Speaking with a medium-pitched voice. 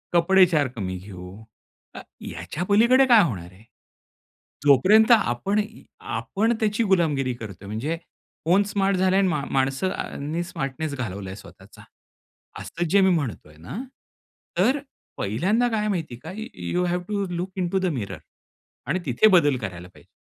Yes: medium, 170 Hz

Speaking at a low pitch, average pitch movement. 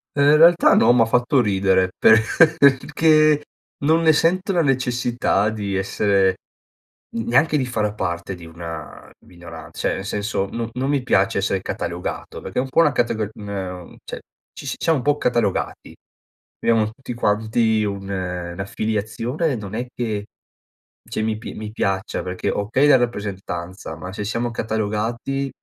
Yes: low, 110 Hz; average, 4.6 semitones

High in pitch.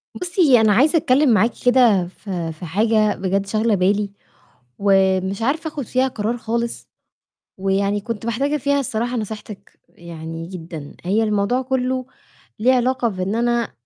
Yes: high, 220 Hz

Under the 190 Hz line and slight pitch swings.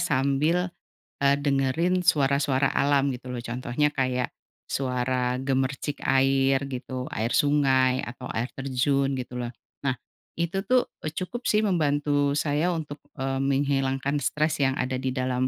Yes: low, 135 Hz; narrow, 2.1 semitones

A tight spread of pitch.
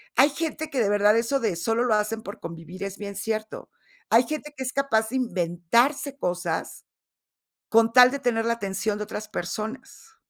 No: average, 4.3 semitones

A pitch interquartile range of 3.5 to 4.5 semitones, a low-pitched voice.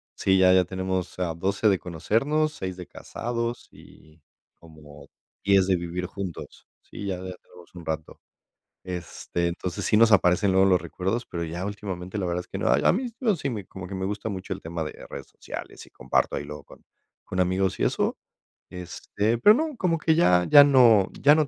Yes: average, 3.9 semitones; very low, 95 Hz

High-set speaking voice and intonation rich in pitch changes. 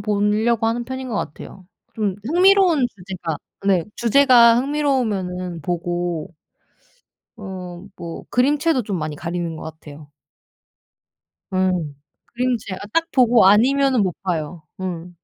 Yes: high, 200 Hz; wide, 6.1 semitones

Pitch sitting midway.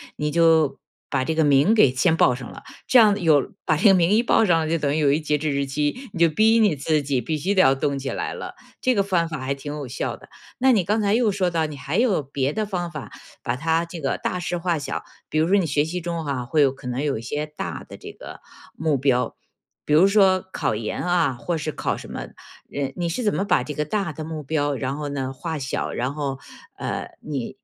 Yes: medium, 155 Hz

